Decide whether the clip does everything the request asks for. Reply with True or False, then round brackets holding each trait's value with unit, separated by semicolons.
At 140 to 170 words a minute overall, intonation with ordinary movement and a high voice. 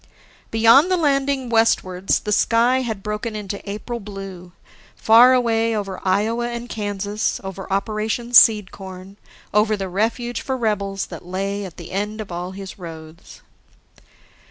True (145 wpm; 3.2 semitones; 210 Hz)